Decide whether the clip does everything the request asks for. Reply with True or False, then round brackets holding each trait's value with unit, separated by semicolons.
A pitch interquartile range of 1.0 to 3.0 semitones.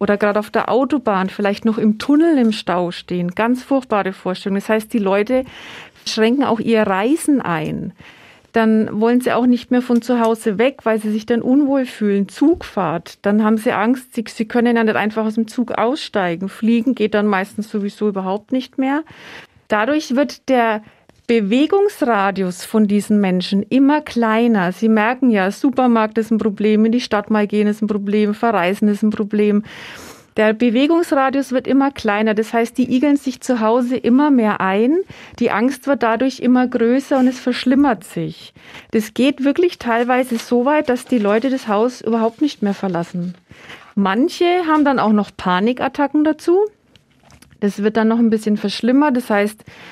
False (3.6 semitones)